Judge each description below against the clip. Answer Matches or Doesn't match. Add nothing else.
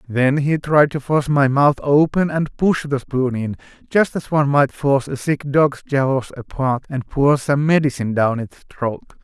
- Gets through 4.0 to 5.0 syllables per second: Matches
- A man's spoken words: Matches